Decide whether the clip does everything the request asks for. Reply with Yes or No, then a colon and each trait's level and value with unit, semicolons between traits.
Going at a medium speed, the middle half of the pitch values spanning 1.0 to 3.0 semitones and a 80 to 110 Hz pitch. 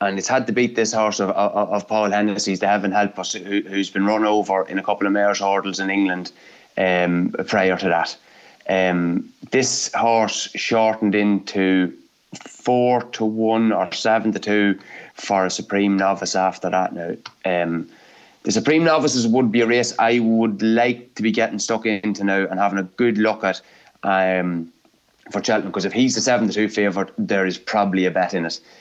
Yes: average, 195 wpm; narrow, 2.6 semitones; low, 100 Hz